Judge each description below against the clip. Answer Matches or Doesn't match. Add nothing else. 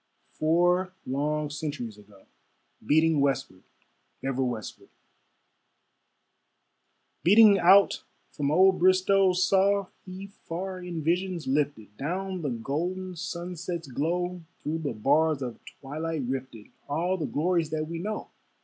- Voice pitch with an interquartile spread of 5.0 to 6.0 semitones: Doesn't match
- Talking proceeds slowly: Matches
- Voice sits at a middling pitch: Matches